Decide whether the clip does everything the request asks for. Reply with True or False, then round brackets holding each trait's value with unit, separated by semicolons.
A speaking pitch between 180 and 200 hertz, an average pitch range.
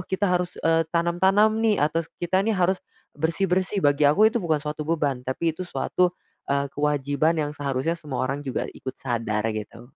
False (160 Hz; 4.3 semitones)